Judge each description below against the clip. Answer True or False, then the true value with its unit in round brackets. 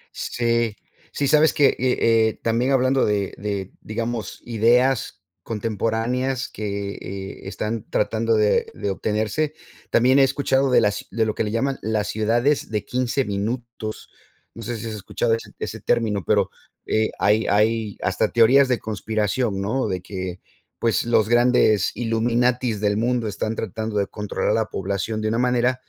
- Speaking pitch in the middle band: False (115 Hz)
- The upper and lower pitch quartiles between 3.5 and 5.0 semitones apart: False (2.7 semitones)